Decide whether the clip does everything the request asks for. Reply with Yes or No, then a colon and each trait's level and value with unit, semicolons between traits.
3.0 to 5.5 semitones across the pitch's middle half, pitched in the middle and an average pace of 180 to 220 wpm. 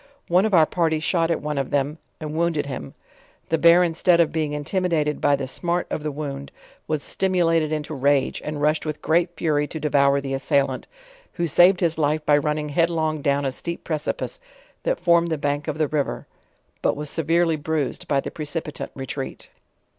No: narrow, 2.5 semitones; medium, 155 Hz; average, 190 wpm